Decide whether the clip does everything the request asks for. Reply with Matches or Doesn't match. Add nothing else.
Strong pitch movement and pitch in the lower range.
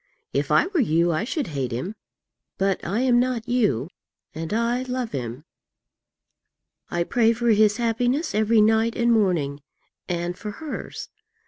Doesn't match